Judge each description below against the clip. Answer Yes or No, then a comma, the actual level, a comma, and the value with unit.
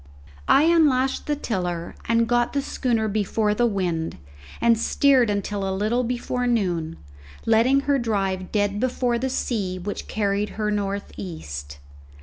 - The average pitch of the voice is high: Yes, high, 215 Hz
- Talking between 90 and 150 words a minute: Yes, average, 145 wpm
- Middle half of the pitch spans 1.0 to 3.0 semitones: No, average, 4.0 semitones